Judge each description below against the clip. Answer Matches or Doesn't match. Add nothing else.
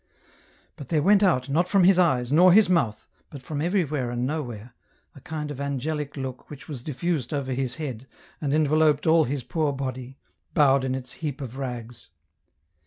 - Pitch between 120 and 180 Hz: Matches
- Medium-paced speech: Matches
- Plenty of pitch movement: Doesn't match